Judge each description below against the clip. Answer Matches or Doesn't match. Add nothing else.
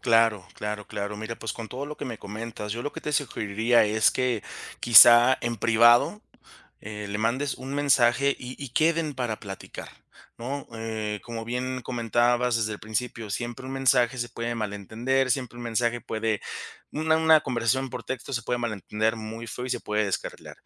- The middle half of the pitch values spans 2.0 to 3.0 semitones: Matches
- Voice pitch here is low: Matches